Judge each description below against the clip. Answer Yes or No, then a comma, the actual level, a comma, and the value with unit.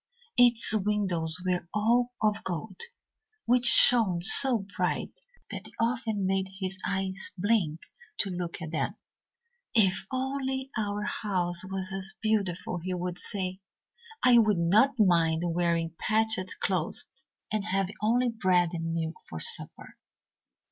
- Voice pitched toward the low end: No, high, 195 Hz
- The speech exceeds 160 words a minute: No, slow, 135 wpm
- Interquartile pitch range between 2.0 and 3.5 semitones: No, average, 4.0 semitones